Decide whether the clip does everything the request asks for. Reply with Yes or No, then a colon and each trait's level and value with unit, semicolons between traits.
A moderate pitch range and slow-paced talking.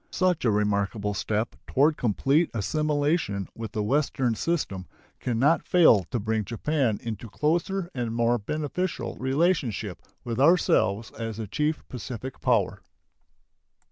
No: wide, 6.1 semitones; slow, 130 wpm